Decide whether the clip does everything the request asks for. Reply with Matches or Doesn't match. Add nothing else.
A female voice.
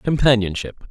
Doesn't match